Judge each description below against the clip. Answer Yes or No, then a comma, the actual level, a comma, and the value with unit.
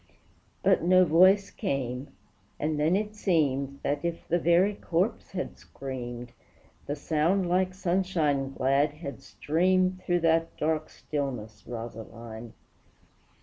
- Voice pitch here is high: No, medium, 155 Hz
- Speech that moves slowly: Yes, slow, 120 wpm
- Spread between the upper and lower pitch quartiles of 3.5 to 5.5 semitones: Yes, average, 5.1 semitones